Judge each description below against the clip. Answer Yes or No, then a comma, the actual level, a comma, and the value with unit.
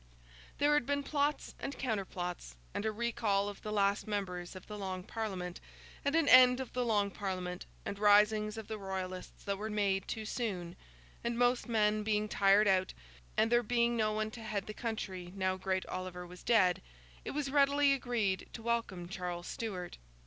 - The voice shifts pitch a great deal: No, average, 3.8 semitones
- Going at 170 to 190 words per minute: Yes, average, 185 wpm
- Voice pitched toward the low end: No, high, 210 Hz